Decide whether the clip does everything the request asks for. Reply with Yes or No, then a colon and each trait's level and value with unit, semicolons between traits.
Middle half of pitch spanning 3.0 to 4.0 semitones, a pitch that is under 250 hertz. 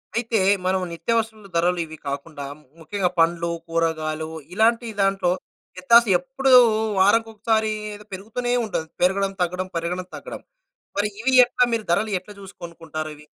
No: average, 4.7 semitones; high, 190 Hz